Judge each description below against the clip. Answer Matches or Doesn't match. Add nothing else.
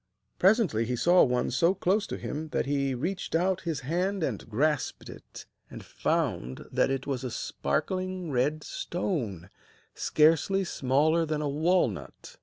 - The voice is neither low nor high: Matches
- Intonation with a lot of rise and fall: Matches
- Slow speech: Doesn't match